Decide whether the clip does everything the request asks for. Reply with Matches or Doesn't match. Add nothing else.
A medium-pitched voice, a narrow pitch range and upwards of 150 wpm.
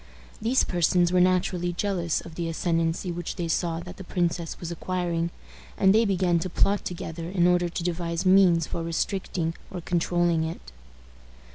Matches